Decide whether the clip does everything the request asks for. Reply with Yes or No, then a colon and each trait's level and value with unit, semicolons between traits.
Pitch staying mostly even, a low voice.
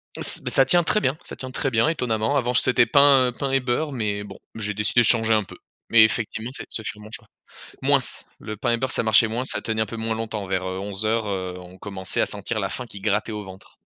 No: average, 3.3 semitones; low, 110 Hz